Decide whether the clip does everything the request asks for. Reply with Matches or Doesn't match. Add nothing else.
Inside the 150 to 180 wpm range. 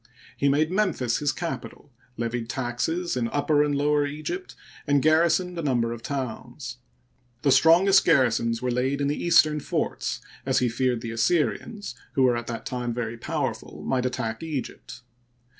Matches